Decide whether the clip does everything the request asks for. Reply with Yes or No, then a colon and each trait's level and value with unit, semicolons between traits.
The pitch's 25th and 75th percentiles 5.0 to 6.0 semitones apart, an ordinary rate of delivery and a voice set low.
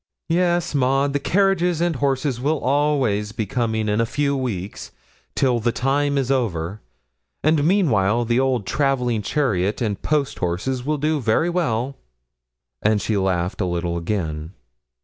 Yes: wide, 5.6 semitones; average, 150 wpm; low, 125 Hz